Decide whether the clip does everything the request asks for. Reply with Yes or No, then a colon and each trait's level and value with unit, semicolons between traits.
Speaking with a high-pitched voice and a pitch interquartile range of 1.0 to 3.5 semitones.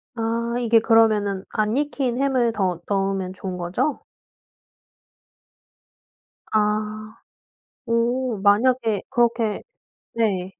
Yes: high, 220 Hz; average, 2.8 semitones